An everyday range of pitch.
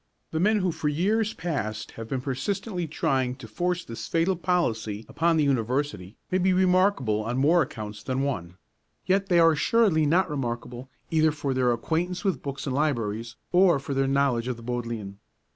No: wide, 6.6 semitones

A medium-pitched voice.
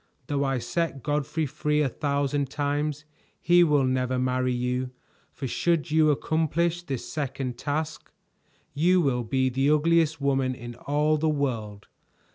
Yes: medium, 145 Hz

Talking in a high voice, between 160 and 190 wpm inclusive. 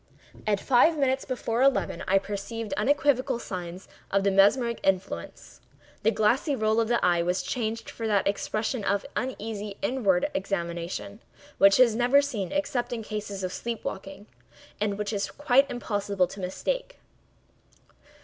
No: high, 215 Hz; average, 150 wpm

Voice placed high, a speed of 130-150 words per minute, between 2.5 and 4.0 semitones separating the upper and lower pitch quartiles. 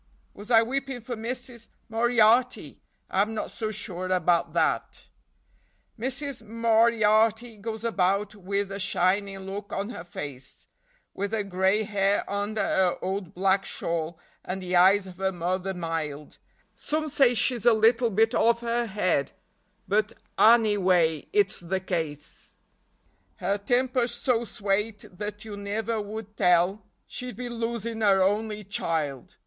Yes: high, 205 Hz; average, 140 wpm; average, 3.4 semitones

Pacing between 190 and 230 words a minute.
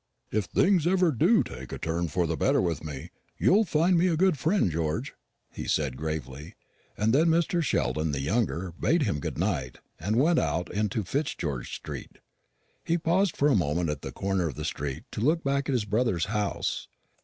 Yes: average, 195 wpm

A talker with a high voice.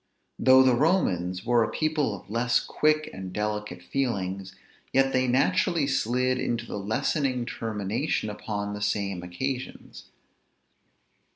No: low, 115 Hz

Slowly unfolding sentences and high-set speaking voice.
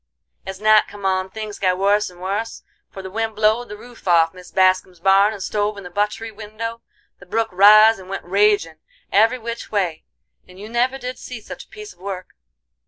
No: fast, 205 wpm; high, 205 Hz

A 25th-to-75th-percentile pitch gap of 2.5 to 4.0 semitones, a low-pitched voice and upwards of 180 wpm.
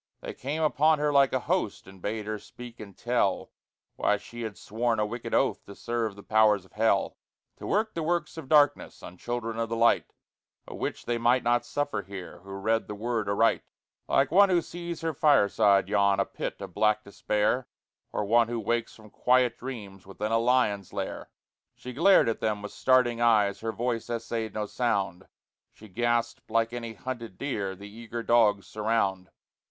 Yes: average, 3.0 semitones; low, 115 Hz; average, 190 wpm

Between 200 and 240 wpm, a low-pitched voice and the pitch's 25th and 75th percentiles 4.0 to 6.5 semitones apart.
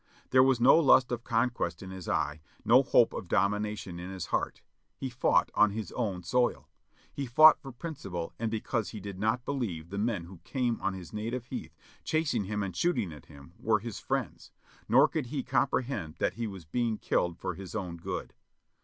Yes: fast, 205 wpm; low, 105 Hz; average, 5.0 semitones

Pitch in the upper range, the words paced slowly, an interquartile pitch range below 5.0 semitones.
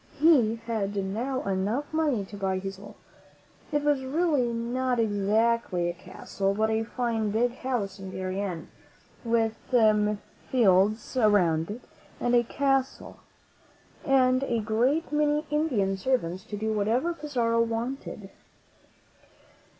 Yes: high, 230 Hz; slow, 120 wpm; average, 4.6 semitones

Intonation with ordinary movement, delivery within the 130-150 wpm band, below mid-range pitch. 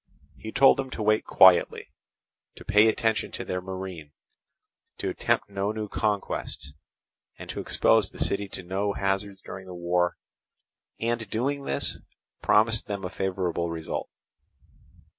Yes: average, 3.0 semitones; average, 140 wpm; low, 100 Hz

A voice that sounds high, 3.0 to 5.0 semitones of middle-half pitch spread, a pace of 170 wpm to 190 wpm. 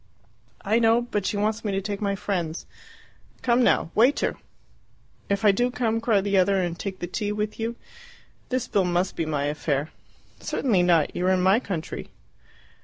Yes: high, 200 Hz; average, 3.7 semitones; average, 180 wpm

